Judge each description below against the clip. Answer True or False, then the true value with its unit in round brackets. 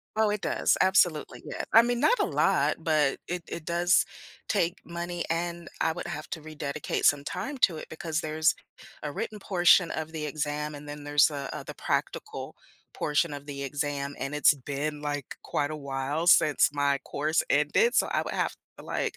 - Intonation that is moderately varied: True (3.0 semitones)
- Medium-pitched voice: True (155 Hz)